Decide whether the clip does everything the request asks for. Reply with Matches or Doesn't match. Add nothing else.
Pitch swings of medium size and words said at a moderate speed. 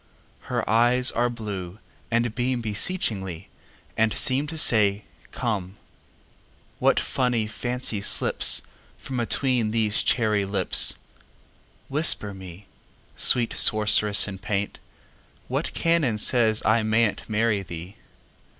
Doesn't match